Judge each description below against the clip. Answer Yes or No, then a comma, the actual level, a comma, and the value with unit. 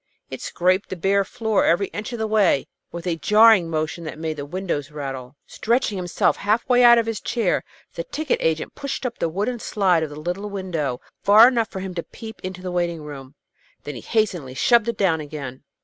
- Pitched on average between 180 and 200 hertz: Yes, medium, 185 Hz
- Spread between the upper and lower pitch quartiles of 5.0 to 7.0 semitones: Yes, wide, 5.5 semitones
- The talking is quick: Yes, fast, 210 wpm